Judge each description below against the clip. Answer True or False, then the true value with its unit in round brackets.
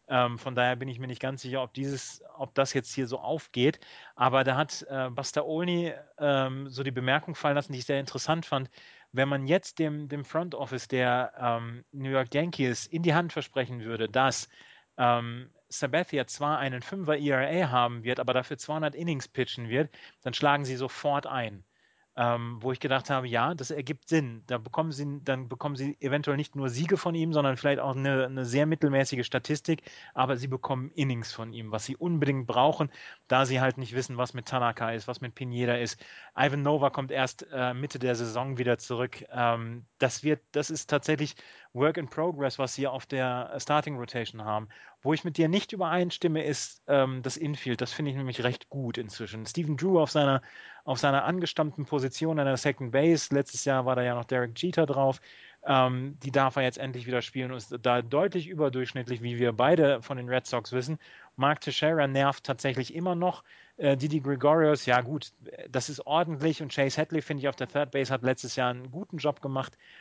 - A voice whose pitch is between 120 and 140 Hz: True (135 Hz)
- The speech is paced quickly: True (200 wpm)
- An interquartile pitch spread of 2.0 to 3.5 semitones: True (2.9 semitones)